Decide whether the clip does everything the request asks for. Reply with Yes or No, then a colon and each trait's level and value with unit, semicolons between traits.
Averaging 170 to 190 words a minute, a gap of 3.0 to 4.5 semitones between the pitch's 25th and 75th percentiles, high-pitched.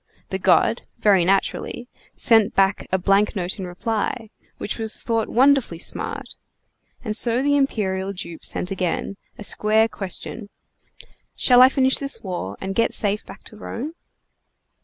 No: average, 150 wpm; average, 3.6 semitones; high, 210 Hz